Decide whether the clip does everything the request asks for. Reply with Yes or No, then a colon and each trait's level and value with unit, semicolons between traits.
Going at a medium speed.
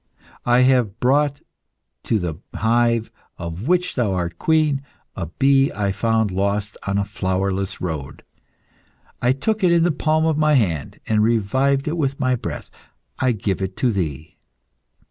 Yes: average, 160 wpm